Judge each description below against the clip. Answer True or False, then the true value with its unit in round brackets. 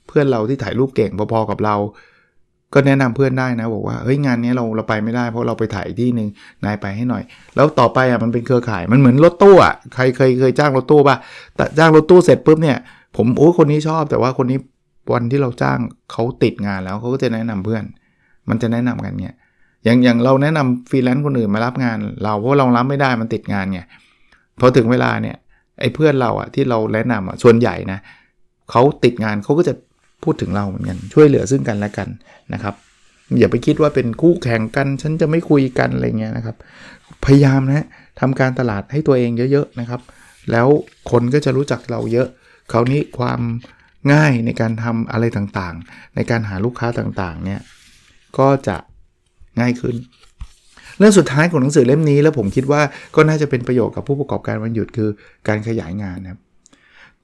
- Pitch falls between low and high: False (120 Hz)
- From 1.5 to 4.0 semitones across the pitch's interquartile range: True (3.7 semitones)